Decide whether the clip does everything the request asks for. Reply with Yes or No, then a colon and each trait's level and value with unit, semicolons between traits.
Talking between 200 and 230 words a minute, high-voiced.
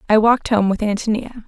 Yes: fast, 205 wpm; high, 220 Hz